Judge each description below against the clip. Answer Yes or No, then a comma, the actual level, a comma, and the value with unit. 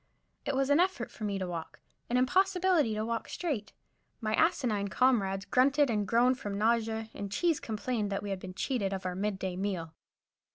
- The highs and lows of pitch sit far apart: No, average, 5.0 semitones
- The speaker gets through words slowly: No, average, 195 wpm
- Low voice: No, high, 220 Hz